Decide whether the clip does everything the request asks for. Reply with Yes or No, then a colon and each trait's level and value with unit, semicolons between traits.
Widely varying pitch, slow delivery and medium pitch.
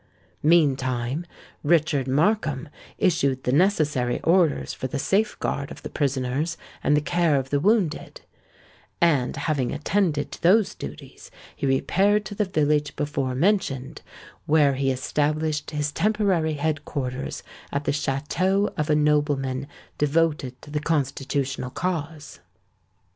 No: average, 3.4 semitones; slow, 130 wpm; medium, 150 Hz